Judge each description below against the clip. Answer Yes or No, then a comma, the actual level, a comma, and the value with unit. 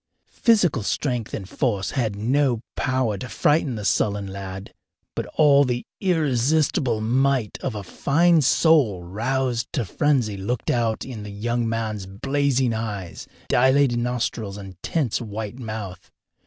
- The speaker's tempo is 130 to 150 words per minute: Yes, average, 140 wpm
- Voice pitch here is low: Yes, low, 120 Hz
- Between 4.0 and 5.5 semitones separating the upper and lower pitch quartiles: Yes, average, 4.6 semitones